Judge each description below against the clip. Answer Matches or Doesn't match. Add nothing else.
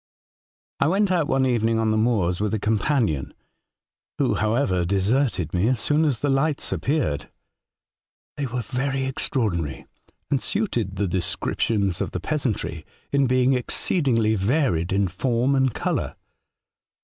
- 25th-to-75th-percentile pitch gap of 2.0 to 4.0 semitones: Doesn't match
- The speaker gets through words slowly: Doesn't match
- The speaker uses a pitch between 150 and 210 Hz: Doesn't match